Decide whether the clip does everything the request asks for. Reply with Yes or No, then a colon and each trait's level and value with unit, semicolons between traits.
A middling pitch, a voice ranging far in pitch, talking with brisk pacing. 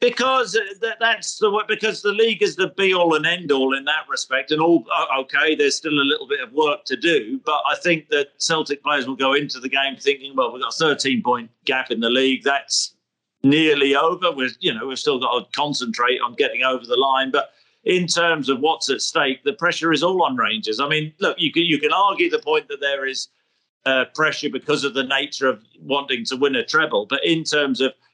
Yes: medium, 150 Hz; wide, 7.4 semitones; fast, 230 wpm